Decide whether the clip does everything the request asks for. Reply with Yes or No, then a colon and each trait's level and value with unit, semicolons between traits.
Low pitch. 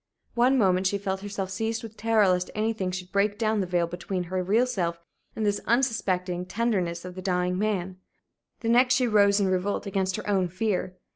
No: high, 195 Hz